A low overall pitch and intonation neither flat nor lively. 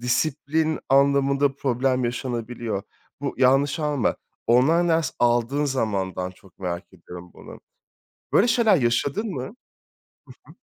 Yes: low, 130 Hz; average, 3.6 semitones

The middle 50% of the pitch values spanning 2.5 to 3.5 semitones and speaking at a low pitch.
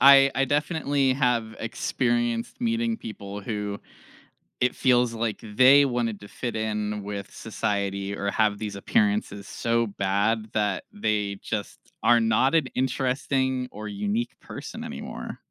No: average, 4.2 semitones; low, 115 Hz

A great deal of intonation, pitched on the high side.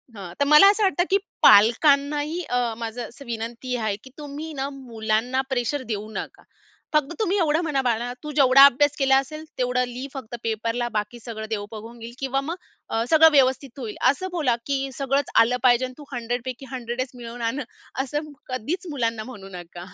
No: average, 3.7 semitones; very high, 255 Hz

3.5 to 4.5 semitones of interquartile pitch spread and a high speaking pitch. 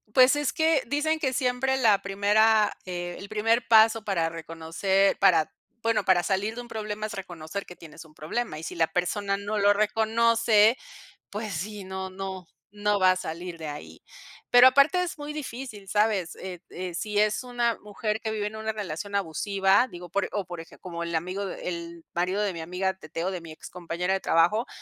Yes: average, 3.8 semitones; high, 200 Hz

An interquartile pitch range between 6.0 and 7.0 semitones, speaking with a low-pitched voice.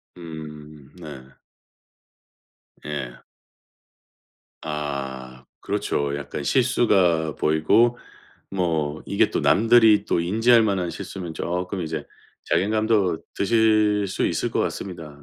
No: wide, 5.6 semitones; very low, 85 Hz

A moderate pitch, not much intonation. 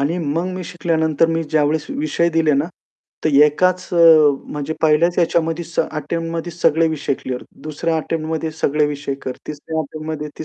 Yes: medium, 160 Hz; narrow, 1.8 semitones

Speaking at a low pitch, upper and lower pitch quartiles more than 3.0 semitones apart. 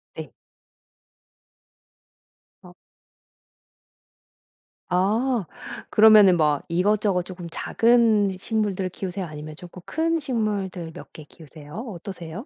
No: high, 190 Hz; average, 3.9 semitones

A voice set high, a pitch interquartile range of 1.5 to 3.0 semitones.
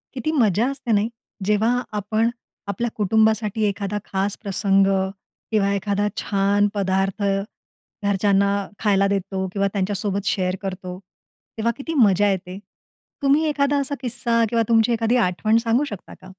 Yes: high, 205 Hz; average, 2.7 semitones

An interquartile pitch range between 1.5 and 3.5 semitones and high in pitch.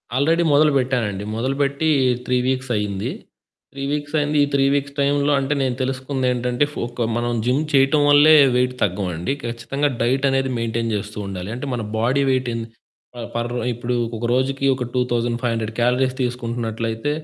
No: average, 2.9 semitones; low, 125 Hz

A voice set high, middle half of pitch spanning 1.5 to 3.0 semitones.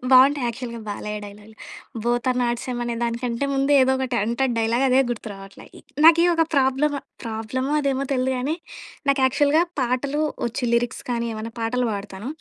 Yes: very high, 250 Hz; narrow, 2.6 semitones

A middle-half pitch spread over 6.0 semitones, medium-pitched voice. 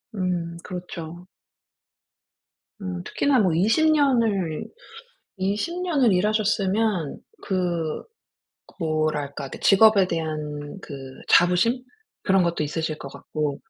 No: average, 5.1 semitones; medium, 180 Hz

